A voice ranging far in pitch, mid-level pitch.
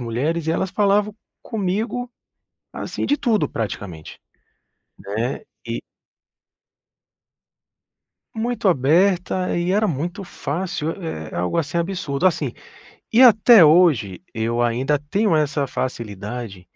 Yes: wide, 8.4 semitones; medium, 165 Hz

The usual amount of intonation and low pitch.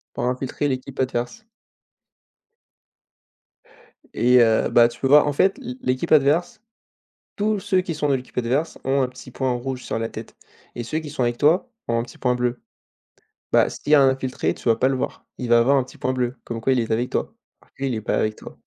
Yes: average, 3.3 semitones; low, 130 Hz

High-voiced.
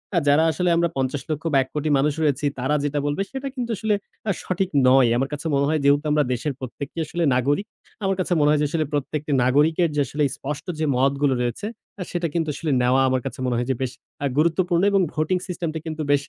No: medium, 150 Hz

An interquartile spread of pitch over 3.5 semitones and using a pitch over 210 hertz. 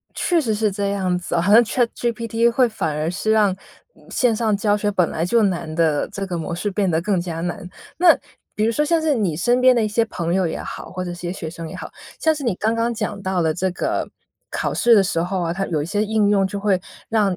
No: average, 4.3 semitones; high, 200 Hz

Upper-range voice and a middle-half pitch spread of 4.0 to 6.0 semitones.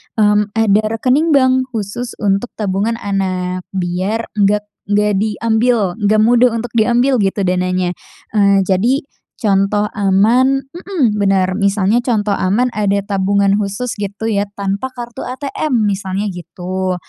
No: high, 205 Hz; average, 3.2 semitones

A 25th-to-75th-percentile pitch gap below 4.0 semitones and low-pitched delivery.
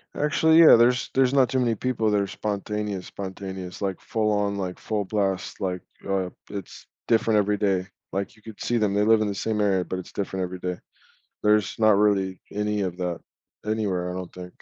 Yes: narrow, 2.5 semitones; low, 100 Hz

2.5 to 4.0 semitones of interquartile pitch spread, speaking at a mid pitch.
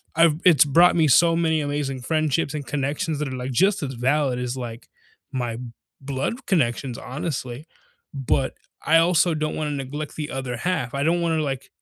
Yes: average, 3.6 semitones; medium, 145 Hz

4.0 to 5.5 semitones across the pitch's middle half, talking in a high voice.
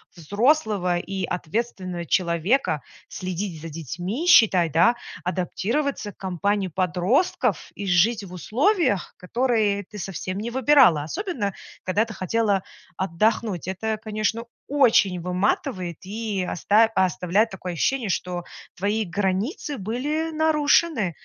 Yes: average, 4.3 semitones; high, 200 Hz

